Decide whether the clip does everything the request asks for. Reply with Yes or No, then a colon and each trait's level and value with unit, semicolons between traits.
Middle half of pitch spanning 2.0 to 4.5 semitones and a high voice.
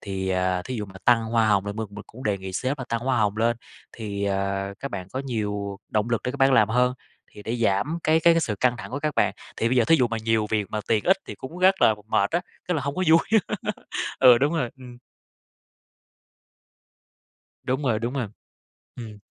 No: average, 4.2 semitones; low, 115 Hz